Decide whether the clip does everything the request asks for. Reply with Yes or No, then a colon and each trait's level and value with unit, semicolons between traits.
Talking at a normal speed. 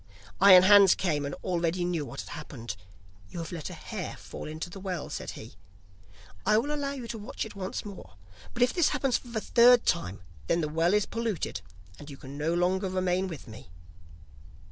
No: fast, 210 wpm